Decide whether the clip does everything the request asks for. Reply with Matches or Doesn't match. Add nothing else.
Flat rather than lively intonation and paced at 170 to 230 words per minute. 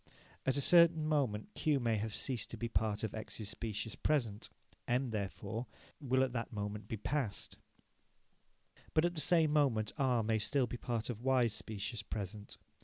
Doesn't match